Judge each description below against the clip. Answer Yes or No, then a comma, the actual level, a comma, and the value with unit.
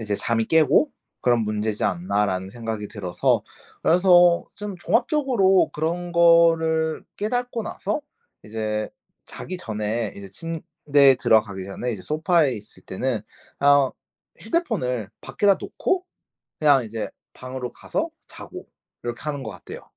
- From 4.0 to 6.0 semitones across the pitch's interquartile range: No, wide, 8.1 semitones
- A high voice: No, low, 135 Hz